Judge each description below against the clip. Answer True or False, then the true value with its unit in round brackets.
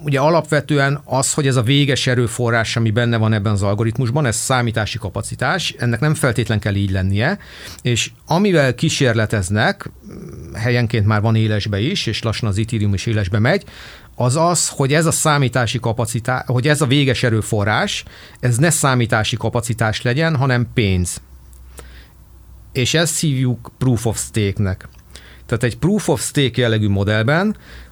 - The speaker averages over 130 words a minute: True (150 wpm)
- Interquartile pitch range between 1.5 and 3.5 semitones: False (4.1 semitones)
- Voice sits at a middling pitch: False (120 Hz)